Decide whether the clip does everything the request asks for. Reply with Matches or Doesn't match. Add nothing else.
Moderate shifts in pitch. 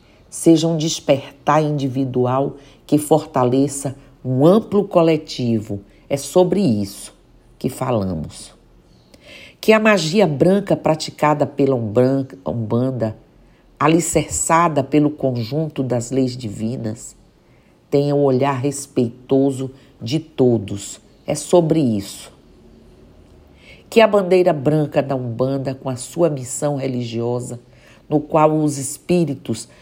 Matches